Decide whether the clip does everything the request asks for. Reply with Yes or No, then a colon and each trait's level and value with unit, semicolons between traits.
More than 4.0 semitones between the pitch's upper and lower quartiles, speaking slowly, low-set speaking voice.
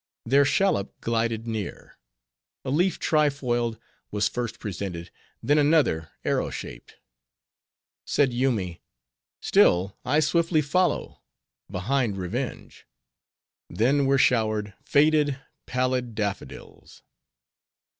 Yes: average, 5.3 semitones; slow, 95 wpm; low, 125 Hz